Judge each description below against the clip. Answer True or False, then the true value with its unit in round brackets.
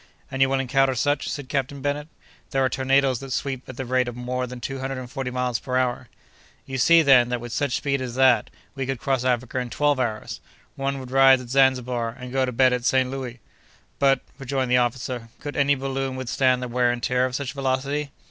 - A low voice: True (130 Hz)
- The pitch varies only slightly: True (1.4 semitones)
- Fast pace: True (225 wpm)